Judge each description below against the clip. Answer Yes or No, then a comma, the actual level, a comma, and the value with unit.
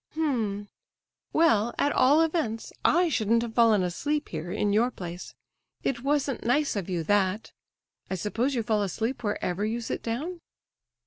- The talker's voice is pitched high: Yes, high, 230 Hz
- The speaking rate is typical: Yes, average, 150 wpm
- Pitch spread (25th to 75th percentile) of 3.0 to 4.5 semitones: No, wide, 5.4 semitones